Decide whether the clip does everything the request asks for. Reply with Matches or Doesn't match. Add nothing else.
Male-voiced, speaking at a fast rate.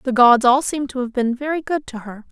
Doesn't match